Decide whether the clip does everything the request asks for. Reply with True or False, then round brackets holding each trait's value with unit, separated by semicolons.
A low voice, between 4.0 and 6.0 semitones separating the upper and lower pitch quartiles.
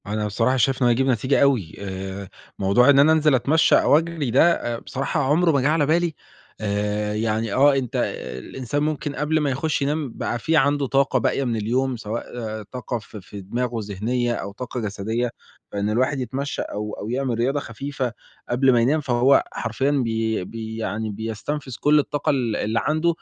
True (125 Hz; 4.3 semitones)